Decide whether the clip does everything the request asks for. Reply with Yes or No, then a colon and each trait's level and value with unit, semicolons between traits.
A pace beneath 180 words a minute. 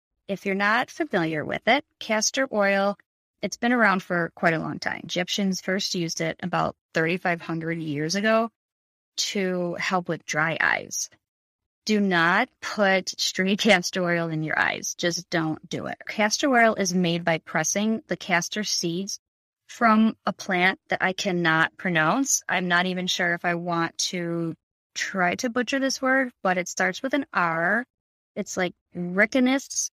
Yes: average, 160 wpm